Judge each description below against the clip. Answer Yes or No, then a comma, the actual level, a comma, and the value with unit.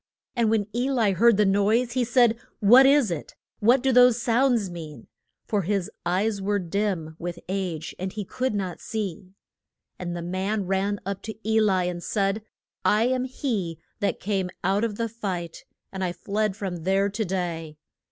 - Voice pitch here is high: Yes, high, 200 Hz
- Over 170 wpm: Yes, average, 180 wpm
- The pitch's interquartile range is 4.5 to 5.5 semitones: No, average, 3.6 semitones